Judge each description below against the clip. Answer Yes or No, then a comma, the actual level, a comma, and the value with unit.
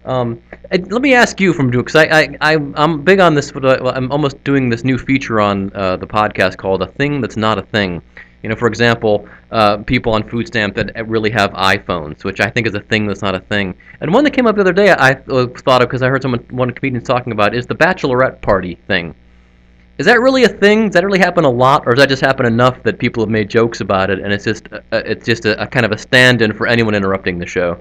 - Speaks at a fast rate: Yes, fast, 260 wpm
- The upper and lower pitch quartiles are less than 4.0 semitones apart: No, average, 5.1 semitones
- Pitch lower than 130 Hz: Yes, low, 120 Hz